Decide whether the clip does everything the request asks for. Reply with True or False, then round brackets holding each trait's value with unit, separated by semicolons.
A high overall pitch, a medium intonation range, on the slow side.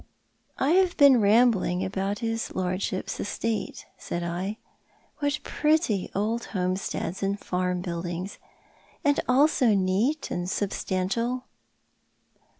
True (200 Hz; 5.0 semitones; 120 wpm)